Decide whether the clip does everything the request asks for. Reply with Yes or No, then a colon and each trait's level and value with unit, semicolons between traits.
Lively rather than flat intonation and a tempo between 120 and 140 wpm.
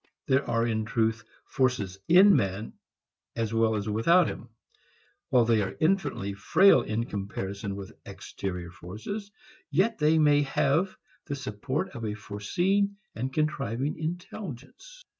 Yes: wide, 7.2 semitones; slow, 135 wpm